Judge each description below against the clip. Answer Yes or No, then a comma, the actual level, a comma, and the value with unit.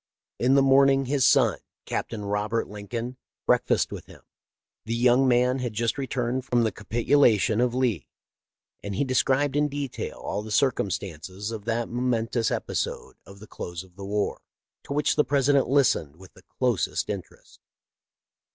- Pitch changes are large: No, average, 4.1 semitones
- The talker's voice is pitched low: Yes, low, 120 Hz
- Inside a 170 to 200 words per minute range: No, average, 160 wpm